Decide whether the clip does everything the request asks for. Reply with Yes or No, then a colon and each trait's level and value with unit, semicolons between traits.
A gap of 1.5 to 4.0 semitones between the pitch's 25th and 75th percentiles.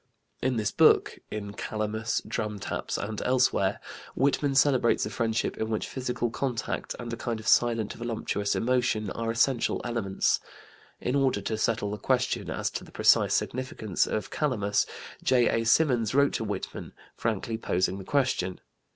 Yes: average, 3.0 semitones